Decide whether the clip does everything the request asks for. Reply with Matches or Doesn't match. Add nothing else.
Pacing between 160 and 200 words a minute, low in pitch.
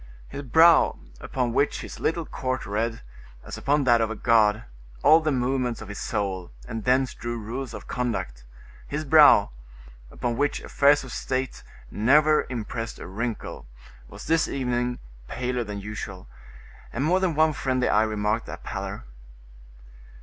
Doesn't match